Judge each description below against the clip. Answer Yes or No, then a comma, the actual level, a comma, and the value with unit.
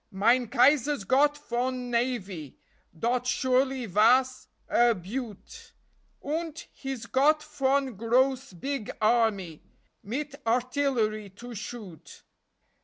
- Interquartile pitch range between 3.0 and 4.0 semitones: Yes, average, 3.7 semitones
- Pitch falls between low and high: No, high, 245 Hz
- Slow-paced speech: Yes, slow, 100 wpm